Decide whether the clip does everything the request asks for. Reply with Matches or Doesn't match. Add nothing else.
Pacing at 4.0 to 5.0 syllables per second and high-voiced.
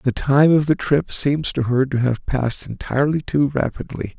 Doesn't match